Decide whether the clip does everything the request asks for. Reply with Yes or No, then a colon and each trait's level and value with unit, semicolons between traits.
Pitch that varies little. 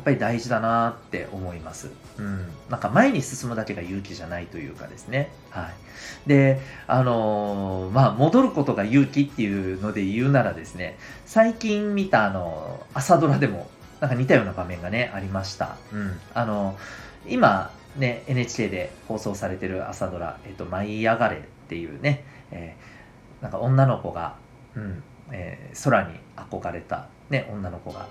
No: wide, 5.7 semitones